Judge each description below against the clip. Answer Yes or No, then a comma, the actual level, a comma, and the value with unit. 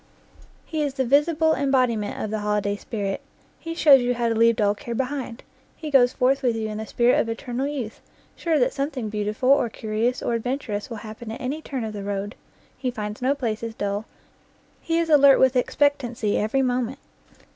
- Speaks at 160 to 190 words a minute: No, average, 200 wpm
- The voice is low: No, high, 245 Hz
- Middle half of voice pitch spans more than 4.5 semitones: No, average, 4.1 semitones